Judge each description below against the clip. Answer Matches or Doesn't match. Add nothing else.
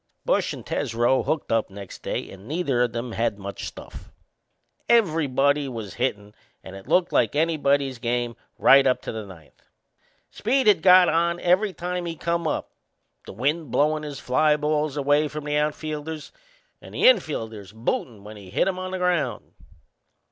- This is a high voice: Doesn't match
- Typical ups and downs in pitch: Doesn't match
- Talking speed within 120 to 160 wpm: Doesn't match